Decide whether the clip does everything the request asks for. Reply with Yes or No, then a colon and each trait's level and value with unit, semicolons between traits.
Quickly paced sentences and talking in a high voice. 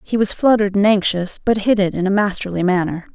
Yes: fast, 230 wpm; high, 200 Hz